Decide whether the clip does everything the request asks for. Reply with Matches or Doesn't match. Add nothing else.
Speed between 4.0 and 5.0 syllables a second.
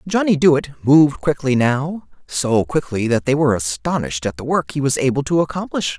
Doesn't match